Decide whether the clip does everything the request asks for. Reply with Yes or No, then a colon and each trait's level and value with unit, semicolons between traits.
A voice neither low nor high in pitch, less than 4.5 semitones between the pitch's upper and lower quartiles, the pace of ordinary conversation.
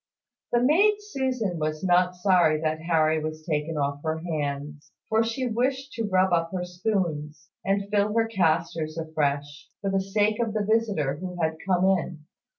No: medium, 180 Hz; average, 5.2 semitones; average, 170 wpm